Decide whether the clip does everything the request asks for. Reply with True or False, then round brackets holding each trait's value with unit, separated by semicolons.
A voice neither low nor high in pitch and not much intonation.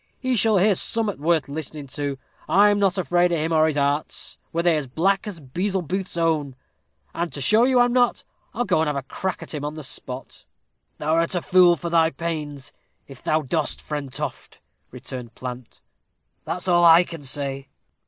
False (165 Hz; 4.3 semitones)